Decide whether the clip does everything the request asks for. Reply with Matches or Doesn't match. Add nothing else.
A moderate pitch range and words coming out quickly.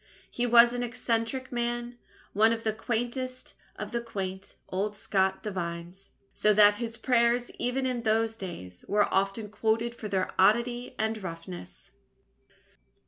Doesn't match